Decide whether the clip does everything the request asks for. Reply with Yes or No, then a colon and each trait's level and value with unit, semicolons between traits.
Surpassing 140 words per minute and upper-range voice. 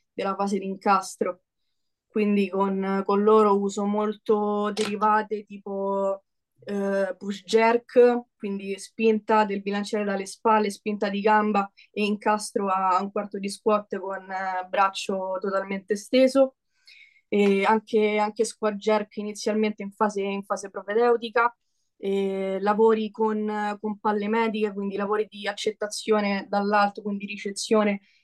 No: average, 125 wpm; high, 210 Hz